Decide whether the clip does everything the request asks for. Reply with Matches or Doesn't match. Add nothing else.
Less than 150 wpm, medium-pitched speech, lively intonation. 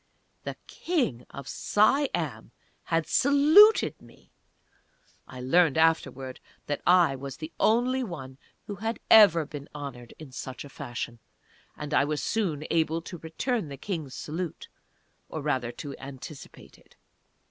Matches